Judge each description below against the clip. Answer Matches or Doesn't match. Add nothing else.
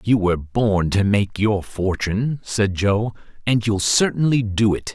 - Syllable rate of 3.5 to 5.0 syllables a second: Matches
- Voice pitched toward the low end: Matches